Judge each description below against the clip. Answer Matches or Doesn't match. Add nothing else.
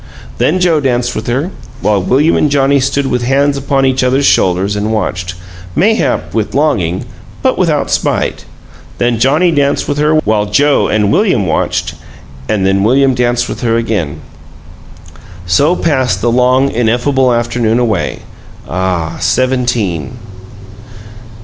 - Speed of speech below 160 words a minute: Matches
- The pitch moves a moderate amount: Matches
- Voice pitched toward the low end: Matches